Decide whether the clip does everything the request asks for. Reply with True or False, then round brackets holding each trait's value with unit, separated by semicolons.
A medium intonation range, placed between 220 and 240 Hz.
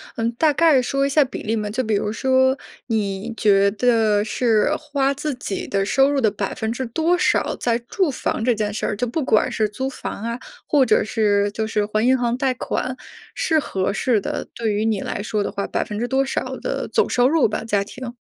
True (3.9 semitones; 235 Hz)